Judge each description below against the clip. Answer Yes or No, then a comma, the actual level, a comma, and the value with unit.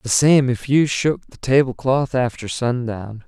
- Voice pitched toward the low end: Yes, low, 125 Hz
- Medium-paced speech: Yes, average, 185 wpm